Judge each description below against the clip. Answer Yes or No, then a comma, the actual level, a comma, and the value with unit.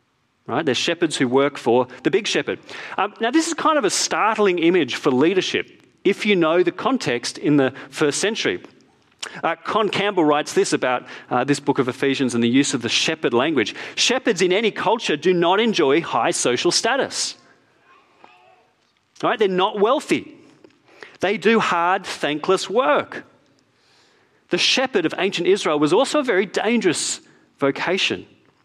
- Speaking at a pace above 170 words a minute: No, average, 160 wpm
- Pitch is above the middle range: No, medium, 175 Hz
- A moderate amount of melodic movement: No, wide, 8.3 semitones